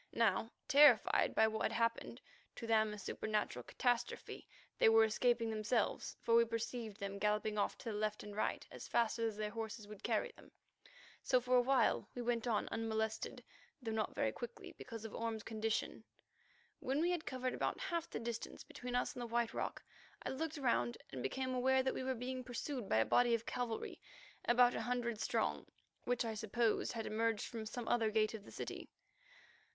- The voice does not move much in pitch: Yes, narrow, 2.3 semitones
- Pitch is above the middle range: Yes, high, 230 Hz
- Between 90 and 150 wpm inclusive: No, average, 190 wpm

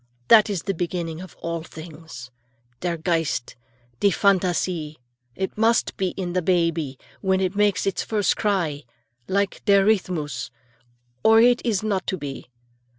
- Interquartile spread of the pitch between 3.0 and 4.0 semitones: Yes, average, 3.5 semitones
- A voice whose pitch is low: No, medium, 185 Hz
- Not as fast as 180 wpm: Yes, average, 150 wpm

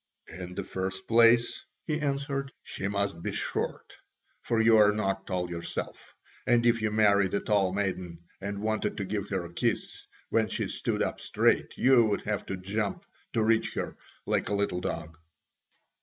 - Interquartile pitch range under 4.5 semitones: Yes, average, 3.1 semitones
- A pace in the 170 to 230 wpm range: Yes, average, 175 wpm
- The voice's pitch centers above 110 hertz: No, low, 100 Hz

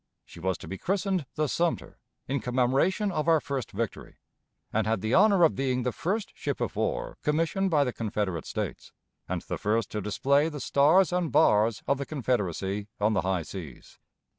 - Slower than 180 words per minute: No, average, 190 wpm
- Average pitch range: No, wide, 7.7 semitones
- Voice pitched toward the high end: No, low, 135 Hz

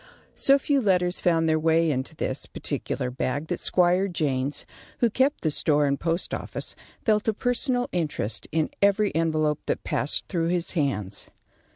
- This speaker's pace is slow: No, average, 165 wpm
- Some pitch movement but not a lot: Yes, average, 5.0 semitones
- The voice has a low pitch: No, medium, 165 Hz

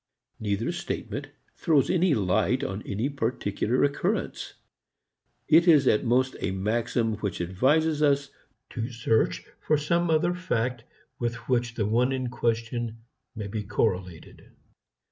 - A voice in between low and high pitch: No, low, 120 Hz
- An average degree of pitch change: Yes, average, 4.6 semitones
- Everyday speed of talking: No, slow, 130 wpm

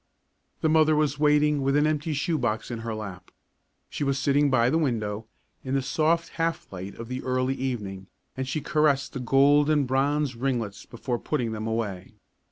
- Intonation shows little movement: No, average, 4.3 semitones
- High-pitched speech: No, low, 135 Hz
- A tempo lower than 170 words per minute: No, average, 180 wpm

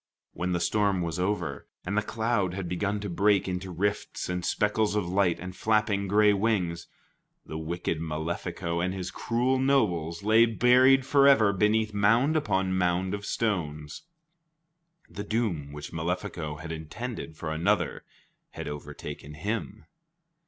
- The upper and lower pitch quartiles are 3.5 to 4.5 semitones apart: Yes, average, 4.0 semitones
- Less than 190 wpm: Yes, average, 145 wpm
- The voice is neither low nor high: No, very low, 95 Hz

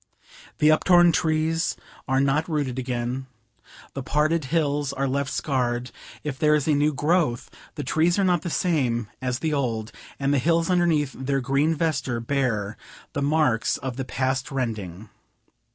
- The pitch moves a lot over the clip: No, average, 3.5 semitones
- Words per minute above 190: No, average, 160 wpm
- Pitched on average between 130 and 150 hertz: Yes, medium, 140 Hz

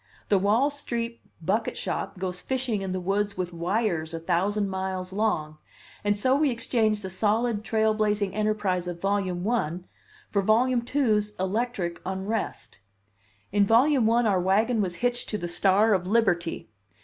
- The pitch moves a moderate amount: Yes, average, 3.5 semitones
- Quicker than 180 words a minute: No, average, 155 wpm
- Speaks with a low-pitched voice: No, high, 205 Hz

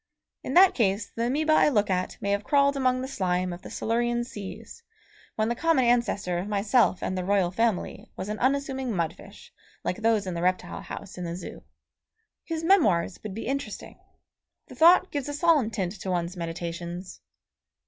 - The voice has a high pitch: Yes, high, 215 Hz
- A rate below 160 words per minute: No, average, 190 wpm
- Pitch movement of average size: No, wide, 6.4 semitones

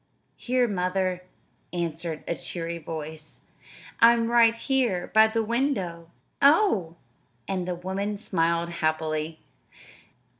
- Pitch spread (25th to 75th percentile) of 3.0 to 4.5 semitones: No, wide, 5.4 semitones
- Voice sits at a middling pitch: Yes, medium, 180 Hz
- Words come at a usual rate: No, slow, 105 wpm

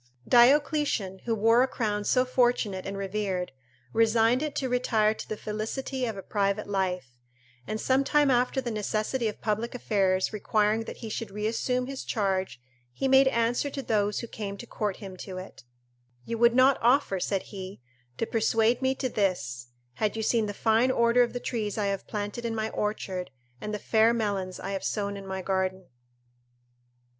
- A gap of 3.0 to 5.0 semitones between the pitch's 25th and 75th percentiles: Yes, average, 3.4 semitones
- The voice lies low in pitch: No, high, 215 Hz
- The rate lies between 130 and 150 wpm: No, average, 185 wpm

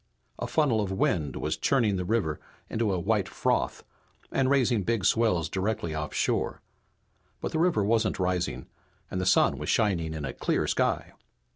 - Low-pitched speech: Yes, low, 100 Hz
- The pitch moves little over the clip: No, average, 4.4 semitones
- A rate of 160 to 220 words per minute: Yes, average, 165 wpm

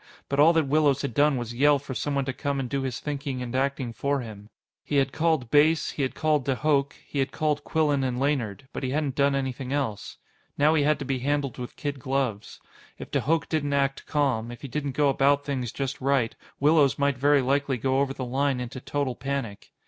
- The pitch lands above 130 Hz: Yes, medium, 140 Hz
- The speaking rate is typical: No, fast, 225 wpm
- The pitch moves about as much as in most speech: No, narrow, 1.9 semitones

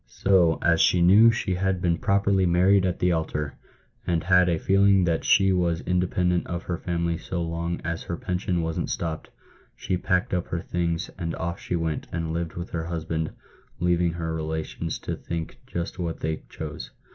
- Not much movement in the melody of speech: Yes, narrow, 1.7 semitones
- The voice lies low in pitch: Yes, very low, 85 Hz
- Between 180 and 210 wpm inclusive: Yes, average, 185 wpm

